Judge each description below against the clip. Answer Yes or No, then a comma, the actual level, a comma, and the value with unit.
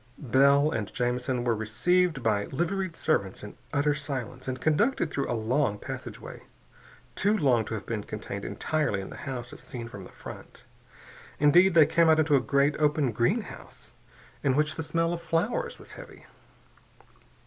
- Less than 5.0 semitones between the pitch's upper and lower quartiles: No, average, 5.3 semitones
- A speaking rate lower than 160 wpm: No, average, 170 wpm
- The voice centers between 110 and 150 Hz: Yes, medium, 140 Hz